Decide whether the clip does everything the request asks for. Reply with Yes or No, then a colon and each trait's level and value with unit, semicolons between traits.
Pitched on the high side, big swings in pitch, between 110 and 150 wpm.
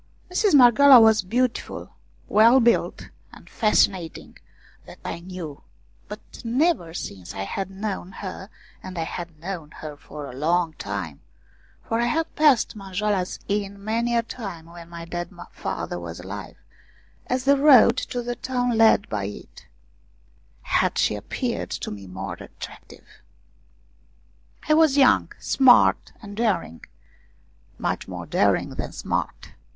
Yes: high, 200 Hz; wide, 6.5 semitones; average, 140 wpm